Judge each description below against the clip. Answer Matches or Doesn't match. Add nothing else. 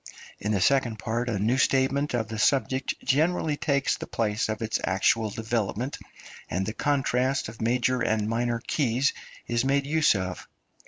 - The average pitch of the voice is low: Matches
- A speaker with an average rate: Matches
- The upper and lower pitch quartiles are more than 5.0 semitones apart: Doesn't match